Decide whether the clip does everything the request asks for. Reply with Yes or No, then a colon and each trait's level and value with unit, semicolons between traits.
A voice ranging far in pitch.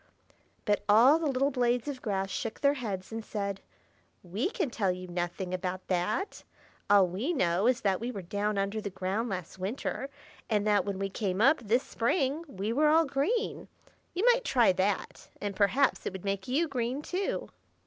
Yes: wide, 5.9 semitones